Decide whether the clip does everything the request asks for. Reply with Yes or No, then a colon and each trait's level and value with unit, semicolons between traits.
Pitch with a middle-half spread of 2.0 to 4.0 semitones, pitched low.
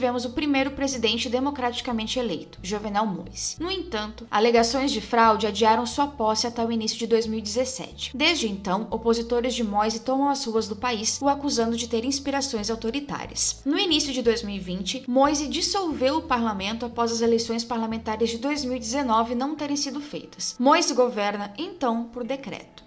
No: average, 3.5 semitones; high, 240 Hz